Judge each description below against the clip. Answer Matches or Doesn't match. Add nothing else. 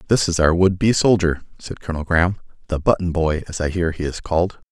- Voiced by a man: Matches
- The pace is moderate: Doesn't match